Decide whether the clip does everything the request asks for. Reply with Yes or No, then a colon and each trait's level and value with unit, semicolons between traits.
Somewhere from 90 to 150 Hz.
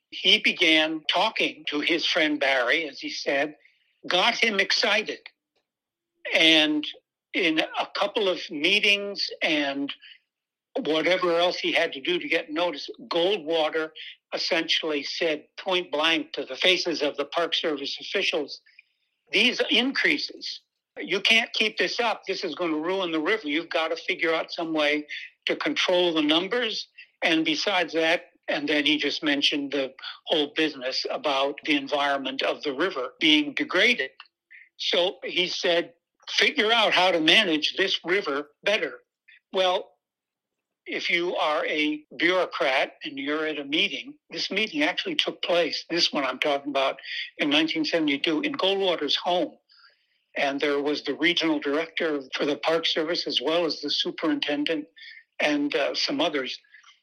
No: medium, 170 Hz